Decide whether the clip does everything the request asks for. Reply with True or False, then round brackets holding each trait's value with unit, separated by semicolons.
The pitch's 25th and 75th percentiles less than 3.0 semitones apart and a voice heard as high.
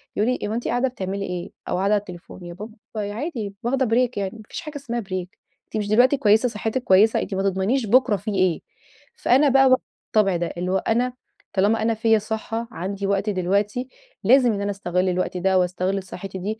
False (3.7 semitones; 205 Hz)